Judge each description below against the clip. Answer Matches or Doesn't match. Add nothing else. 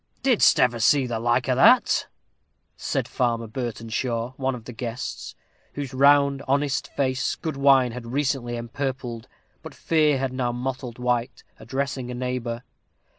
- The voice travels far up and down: Doesn't match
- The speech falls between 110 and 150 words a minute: Matches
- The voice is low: Matches